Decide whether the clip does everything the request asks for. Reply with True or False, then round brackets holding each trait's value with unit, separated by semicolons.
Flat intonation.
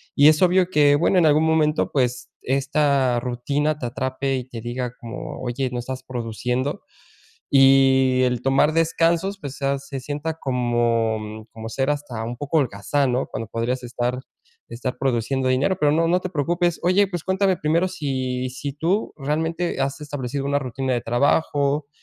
False (3.5 semitones)